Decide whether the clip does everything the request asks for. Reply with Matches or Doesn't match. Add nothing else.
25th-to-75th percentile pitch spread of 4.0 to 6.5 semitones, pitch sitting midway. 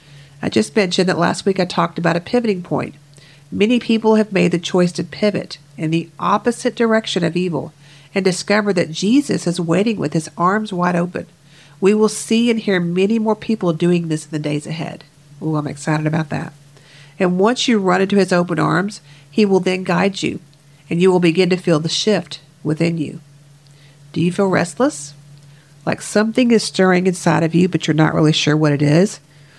Matches